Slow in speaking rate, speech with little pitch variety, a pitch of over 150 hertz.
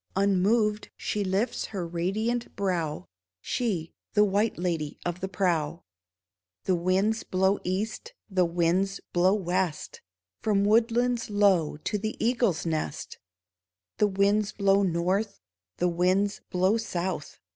No: slow, 125 wpm; average, 3.2 semitones; high, 190 Hz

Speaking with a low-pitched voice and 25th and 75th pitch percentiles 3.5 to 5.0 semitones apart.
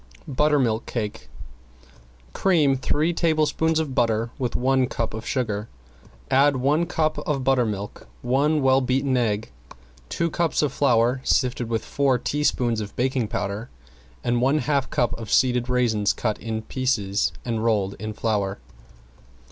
Yes: low, 125 Hz; average, 3.9 semitones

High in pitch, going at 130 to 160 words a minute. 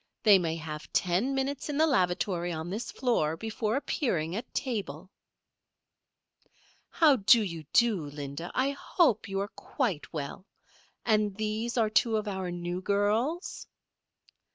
Yes: high, 205 Hz; average, 140 wpm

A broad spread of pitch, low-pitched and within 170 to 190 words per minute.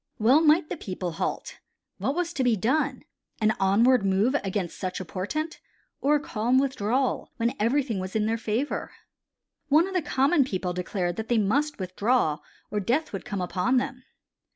No: wide, 6.0 semitones; high, 230 Hz; average, 175 wpm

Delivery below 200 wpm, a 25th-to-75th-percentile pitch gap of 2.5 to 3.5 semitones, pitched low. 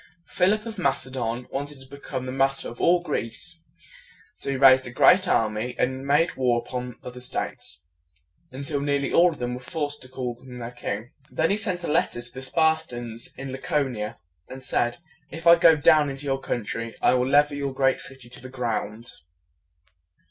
No: fast, 205 wpm; average, 3.1 semitones; low, 130 Hz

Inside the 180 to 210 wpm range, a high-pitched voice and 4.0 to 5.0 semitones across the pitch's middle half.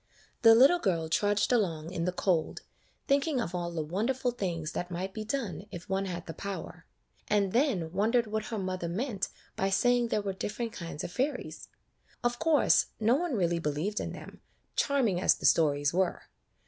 No: average, 185 wpm; high, 195 Hz; wide, 5.5 semitones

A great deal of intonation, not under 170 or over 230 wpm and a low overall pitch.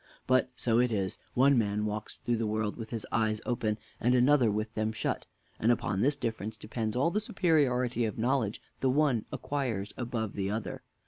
No: average, 2.9 semitones; average, 190 wpm; low, 115 Hz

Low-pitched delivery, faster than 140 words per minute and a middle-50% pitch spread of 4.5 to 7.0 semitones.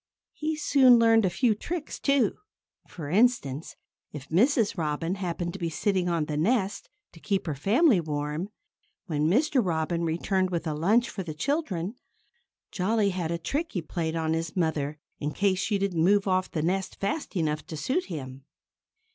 No: medium, 180 Hz; average, 180 wpm; average, 5.1 semitones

